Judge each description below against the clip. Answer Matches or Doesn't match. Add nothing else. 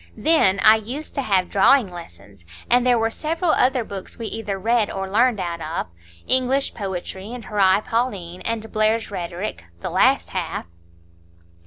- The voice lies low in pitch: Doesn't match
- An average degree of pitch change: Matches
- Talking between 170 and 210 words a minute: Doesn't match